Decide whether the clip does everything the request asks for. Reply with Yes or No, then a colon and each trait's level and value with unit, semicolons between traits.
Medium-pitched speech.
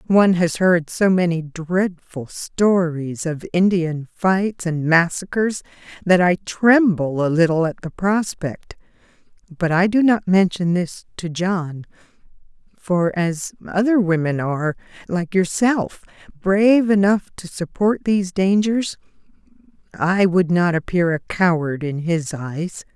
Yes: medium, 180 Hz